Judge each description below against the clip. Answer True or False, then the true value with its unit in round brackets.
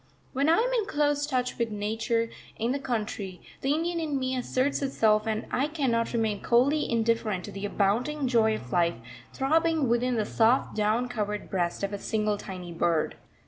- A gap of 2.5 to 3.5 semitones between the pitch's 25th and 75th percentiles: False (4.7 semitones)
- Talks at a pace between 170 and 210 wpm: True (185 wpm)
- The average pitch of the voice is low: False (235 Hz)